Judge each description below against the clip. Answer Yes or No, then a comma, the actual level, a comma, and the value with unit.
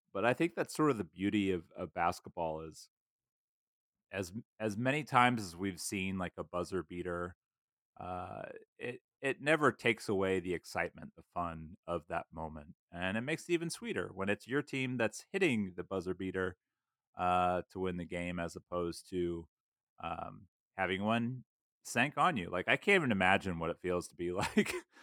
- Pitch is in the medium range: No, very low, 95 Hz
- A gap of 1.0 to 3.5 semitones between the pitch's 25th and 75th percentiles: No, average, 4.3 semitones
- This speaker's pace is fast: No, average, 180 wpm